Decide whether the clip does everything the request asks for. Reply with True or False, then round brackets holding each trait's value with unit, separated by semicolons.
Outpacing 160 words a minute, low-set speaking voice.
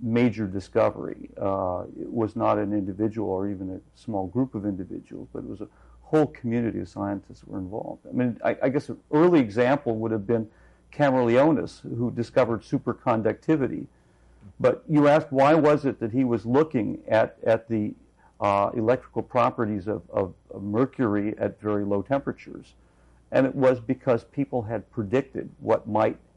True (170 wpm; 115 Hz)